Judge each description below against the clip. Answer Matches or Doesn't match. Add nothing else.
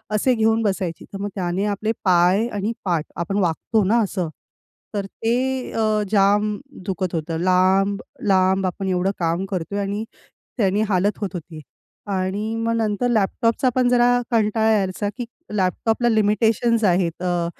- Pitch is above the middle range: Matches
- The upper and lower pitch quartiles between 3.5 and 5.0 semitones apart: Doesn't match